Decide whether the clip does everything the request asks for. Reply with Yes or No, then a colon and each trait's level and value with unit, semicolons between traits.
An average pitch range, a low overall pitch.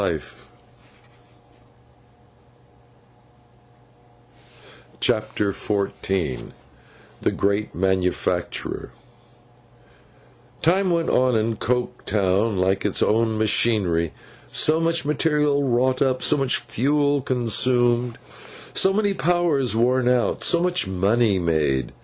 No: wide, 6.1 semitones; low, 120 Hz